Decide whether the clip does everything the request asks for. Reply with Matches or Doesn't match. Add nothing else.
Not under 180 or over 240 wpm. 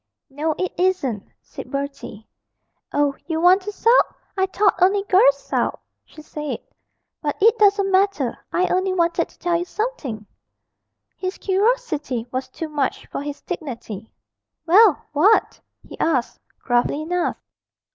Doesn't match